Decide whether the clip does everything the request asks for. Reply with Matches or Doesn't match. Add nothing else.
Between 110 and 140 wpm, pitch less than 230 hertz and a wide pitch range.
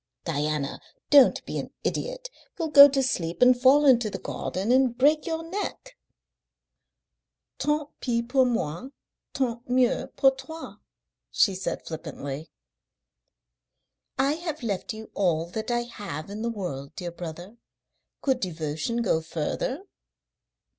Doesn't match